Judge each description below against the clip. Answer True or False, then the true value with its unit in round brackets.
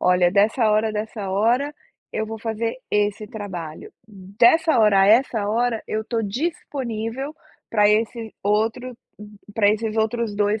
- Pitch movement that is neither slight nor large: False (2.0 semitones)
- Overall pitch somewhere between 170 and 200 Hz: False (220 Hz)